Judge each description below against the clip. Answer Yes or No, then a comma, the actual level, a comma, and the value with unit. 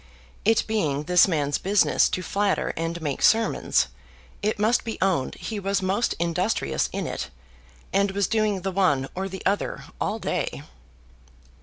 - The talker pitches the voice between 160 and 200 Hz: Yes, high, 190 Hz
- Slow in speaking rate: No, average, 155 wpm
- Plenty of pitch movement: No, average, 3.5 semitones